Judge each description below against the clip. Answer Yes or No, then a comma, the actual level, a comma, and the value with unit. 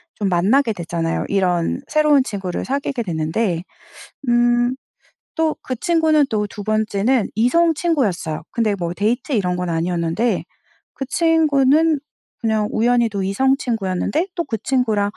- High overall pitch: Yes, high, 225 Hz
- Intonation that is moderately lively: No, wide, 6.2 semitones